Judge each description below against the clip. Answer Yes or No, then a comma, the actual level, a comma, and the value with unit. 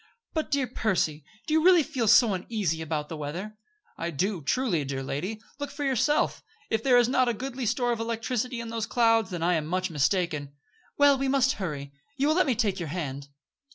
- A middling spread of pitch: No, wide, 7.7 semitones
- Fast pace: Yes, fast, 210 wpm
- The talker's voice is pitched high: Yes, high, 215 Hz